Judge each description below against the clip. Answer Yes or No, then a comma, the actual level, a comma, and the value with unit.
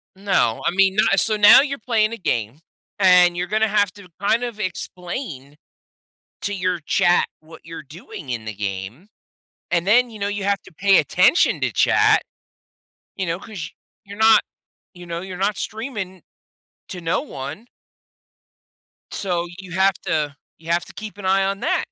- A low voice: No, high, 190 Hz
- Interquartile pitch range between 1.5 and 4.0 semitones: Yes, average, 3.6 semitones